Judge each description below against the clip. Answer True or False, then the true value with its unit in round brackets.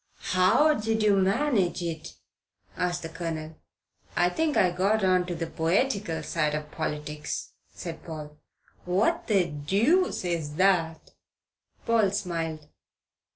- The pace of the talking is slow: True (125 wpm)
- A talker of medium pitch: True (180 Hz)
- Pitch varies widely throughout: False (4.0 semitones)